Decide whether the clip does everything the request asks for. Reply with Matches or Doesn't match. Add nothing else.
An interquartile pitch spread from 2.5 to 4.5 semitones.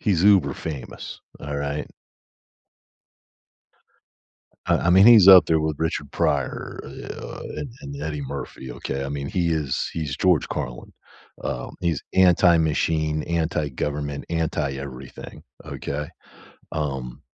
Matches